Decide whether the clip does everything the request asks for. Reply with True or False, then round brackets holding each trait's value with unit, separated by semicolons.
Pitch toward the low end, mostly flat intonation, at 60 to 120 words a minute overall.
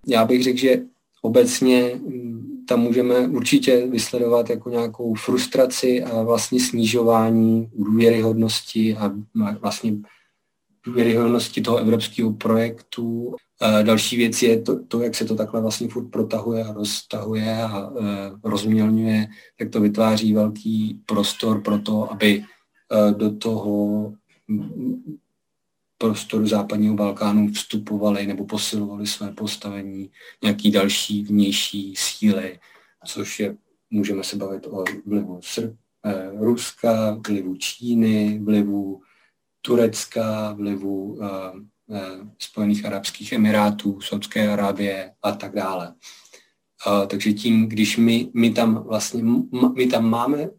True (110 Hz; 2.1 semitones; 115 wpm)